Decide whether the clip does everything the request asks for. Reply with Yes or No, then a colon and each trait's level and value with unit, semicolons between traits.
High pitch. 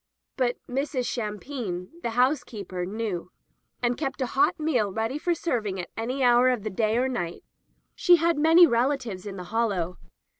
Yes: high, 240 Hz